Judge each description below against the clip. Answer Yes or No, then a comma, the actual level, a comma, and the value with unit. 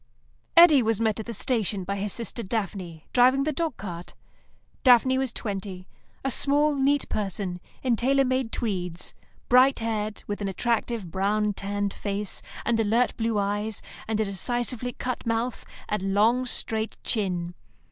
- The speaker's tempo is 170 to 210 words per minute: No, average, 155 wpm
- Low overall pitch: No, high, 220 Hz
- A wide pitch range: No, average, 3.9 semitones